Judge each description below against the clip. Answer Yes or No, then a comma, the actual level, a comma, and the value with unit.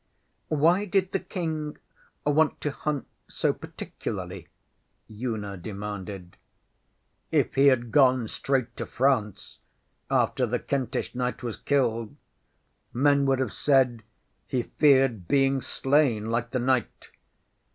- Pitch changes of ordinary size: Yes, average, 3.7 semitones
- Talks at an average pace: No, slow, 120 wpm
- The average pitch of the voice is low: Yes, low, 130 Hz